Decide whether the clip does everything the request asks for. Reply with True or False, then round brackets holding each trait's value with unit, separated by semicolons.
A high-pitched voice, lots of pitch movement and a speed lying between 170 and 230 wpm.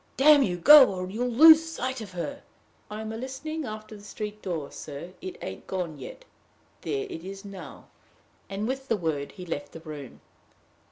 True (210 Hz; 7.0 semitones; 180 wpm)